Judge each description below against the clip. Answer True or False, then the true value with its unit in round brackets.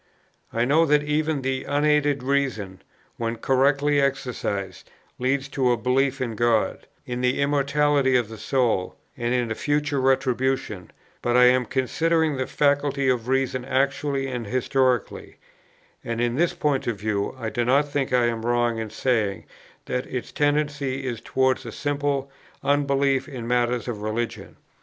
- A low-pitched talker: True (130 Hz)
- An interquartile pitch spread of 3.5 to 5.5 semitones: False (2.8 semitones)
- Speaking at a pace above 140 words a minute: True (155 wpm)